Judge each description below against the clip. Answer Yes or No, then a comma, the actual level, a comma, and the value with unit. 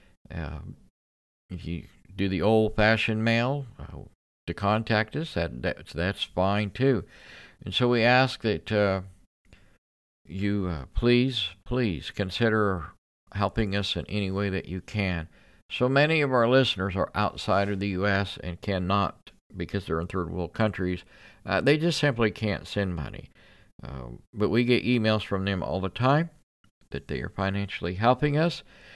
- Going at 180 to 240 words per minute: No, average, 155 wpm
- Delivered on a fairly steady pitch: No, average, 4.1 semitones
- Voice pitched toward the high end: No, low, 100 Hz